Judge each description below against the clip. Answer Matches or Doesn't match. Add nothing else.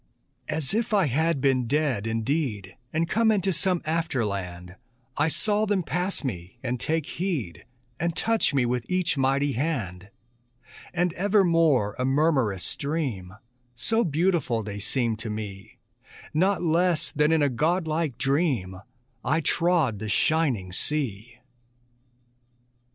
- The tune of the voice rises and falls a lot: Matches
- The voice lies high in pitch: Doesn't match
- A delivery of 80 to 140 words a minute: Matches